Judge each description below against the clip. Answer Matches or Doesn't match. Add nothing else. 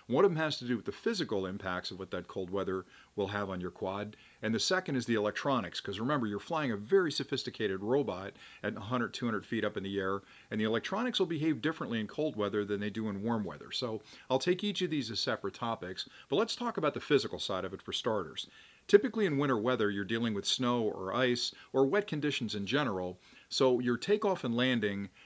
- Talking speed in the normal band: Doesn't match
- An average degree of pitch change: Doesn't match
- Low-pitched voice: Matches